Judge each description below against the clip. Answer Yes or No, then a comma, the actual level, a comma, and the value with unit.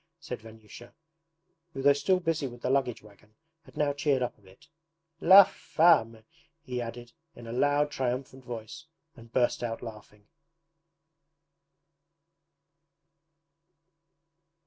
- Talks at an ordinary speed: No, slow, 120 wpm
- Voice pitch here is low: Yes, low, 125 Hz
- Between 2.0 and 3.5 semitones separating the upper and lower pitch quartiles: No, average, 3.9 semitones